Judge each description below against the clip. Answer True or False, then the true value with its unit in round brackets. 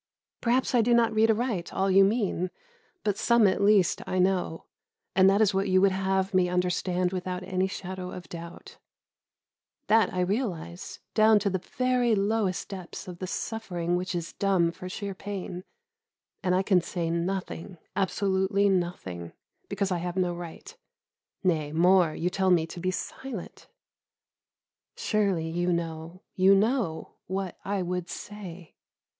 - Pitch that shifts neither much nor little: False (2.2 semitones)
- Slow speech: False (155 wpm)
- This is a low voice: False (185 Hz)